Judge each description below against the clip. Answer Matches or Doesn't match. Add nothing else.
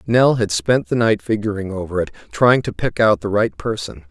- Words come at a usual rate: Doesn't match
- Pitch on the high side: Doesn't match